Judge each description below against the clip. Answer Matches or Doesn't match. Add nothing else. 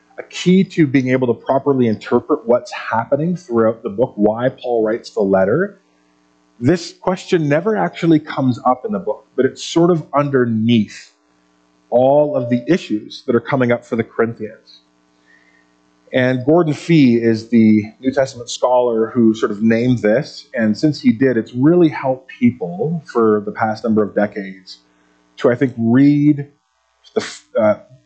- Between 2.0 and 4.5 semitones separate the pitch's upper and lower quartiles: Doesn't match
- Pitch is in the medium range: Doesn't match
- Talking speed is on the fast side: Doesn't match